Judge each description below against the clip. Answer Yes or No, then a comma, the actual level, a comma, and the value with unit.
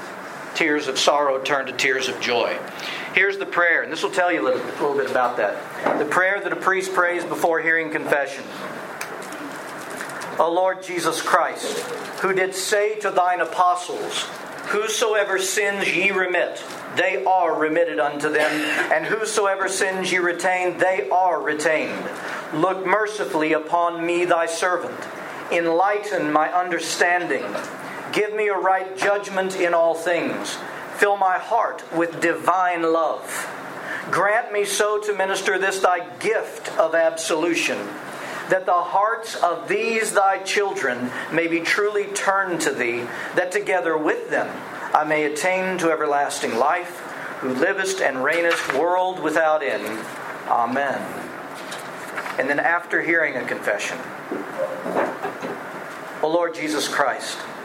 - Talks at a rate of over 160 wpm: No, average, 140 wpm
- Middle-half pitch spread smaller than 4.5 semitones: Yes, average, 2.9 semitones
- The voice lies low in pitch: No, medium, 180 Hz